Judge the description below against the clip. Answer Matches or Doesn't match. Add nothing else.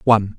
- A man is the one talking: Matches